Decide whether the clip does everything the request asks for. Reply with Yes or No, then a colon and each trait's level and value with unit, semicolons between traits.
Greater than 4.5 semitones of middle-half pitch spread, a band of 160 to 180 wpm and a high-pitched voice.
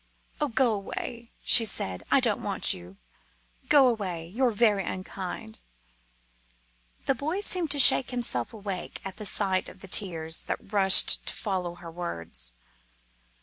No: average, 5.2 semitones; average, 145 wpm; high, 200 Hz